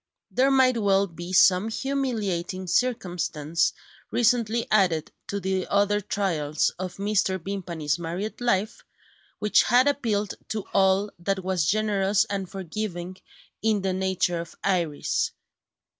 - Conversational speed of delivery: No, slow, 125 wpm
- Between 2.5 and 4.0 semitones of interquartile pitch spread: Yes, average, 3.2 semitones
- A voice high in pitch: Yes, high, 195 Hz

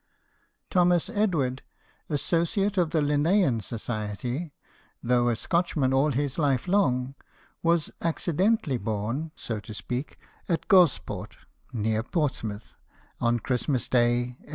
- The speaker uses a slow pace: Yes, slow, 115 wpm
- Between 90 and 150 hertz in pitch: Yes, low, 135 Hz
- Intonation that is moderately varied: No, wide, 5.9 semitones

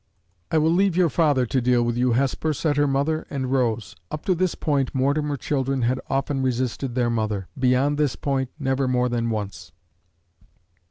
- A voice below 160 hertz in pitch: Yes, low, 135 Hz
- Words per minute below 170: No, average, 180 wpm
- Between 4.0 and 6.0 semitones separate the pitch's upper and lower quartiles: No, average, 2.9 semitones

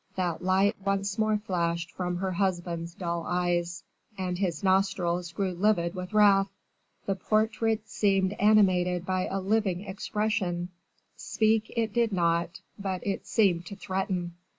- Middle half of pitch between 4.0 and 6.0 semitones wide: No, narrow, 2.6 semitones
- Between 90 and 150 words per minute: Yes, average, 140 wpm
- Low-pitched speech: No, high, 190 Hz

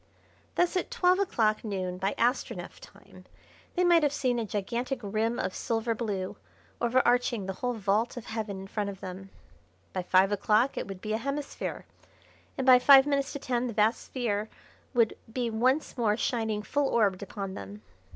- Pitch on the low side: No, high, 225 Hz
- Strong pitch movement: No, average, 4.1 semitones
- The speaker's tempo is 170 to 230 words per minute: Yes, average, 180 wpm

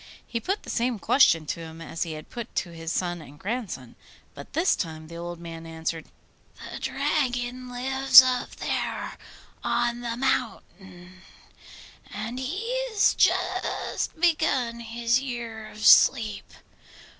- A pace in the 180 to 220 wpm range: No, average, 140 wpm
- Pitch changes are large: Yes, wide, 6.9 semitones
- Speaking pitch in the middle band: No, high, 230 Hz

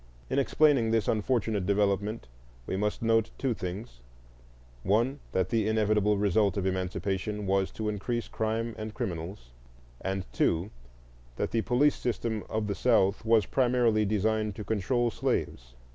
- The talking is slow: No, average, 145 wpm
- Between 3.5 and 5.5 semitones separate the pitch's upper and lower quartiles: No, narrow, 2.6 semitones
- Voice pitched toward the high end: No, low, 105 Hz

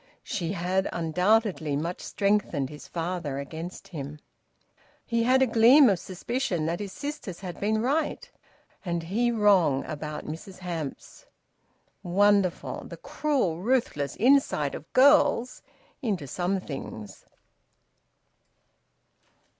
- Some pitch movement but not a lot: No, wide, 5.8 semitones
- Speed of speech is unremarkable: No, slow, 115 wpm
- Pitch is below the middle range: No, medium, 185 Hz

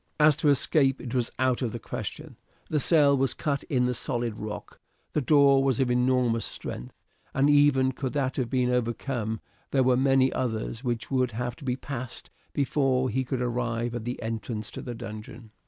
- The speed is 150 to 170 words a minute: No, average, 190 wpm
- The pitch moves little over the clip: Yes, narrow, 2.3 semitones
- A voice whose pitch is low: Yes, low, 125 Hz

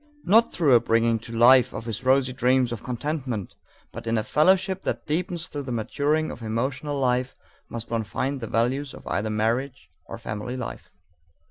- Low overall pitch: Yes, low, 125 Hz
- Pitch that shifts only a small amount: No, average, 3.8 semitones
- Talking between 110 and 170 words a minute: No, average, 185 wpm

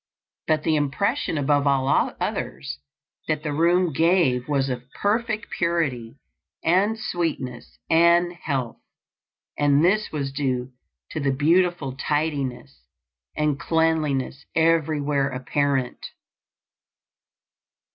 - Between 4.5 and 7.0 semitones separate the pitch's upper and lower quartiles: No, average, 3.7 semitones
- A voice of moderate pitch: Yes, medium, 150 Hz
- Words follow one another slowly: Yes, slow, 100 wpm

